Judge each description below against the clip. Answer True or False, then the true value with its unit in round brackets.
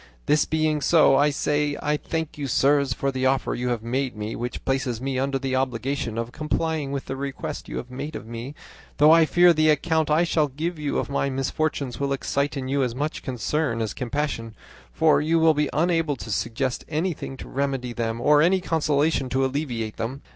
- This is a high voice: False (140 Hz)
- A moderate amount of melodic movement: True (3.1 semitones)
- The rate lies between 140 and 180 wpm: False (205 wpm)